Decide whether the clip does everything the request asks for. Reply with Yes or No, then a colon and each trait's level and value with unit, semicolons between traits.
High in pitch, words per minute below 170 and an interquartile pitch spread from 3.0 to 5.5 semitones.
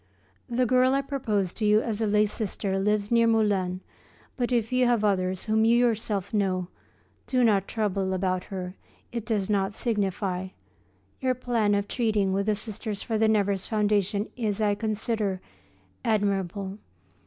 No: high, 210 Hz; average, 160 wpm; narrow, 2.6 semitones